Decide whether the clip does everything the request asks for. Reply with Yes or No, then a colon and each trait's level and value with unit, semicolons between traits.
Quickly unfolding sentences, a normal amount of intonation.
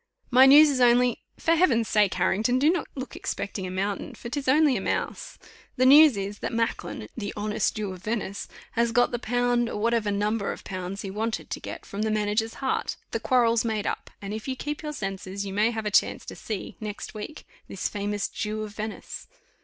Yes: fast, 215 wpm; average, 3.3 semitones